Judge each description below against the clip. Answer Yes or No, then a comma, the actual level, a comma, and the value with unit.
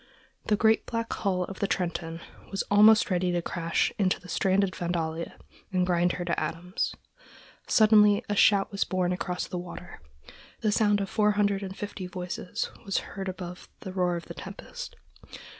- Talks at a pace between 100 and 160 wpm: No, average, 175 wpm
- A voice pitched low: No, medium, 185 Hz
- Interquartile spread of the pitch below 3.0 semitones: Yes, narrow, 2.4 semitones